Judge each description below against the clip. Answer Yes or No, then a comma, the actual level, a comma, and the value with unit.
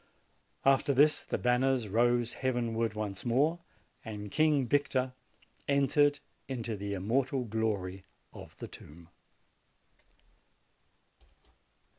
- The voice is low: Yes, low, 120 Hz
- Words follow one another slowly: Yes, slow, 95 wpm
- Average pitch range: Yes, average, 4.1 semitones